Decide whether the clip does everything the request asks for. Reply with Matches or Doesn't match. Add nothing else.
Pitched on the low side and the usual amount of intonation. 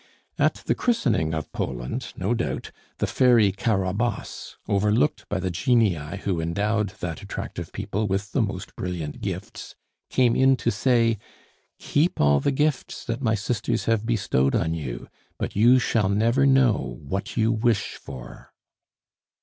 Matches